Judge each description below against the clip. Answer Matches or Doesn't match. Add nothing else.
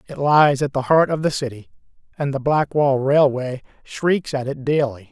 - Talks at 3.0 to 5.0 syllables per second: Matches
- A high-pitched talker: Doesn't match